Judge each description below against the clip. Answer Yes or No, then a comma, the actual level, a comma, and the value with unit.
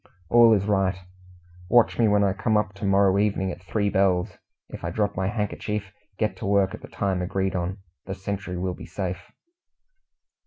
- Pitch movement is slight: Yes, narrow, 1.7 semitones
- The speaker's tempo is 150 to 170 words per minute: No, average, 190 wpm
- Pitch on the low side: Yes, low, 100 Hz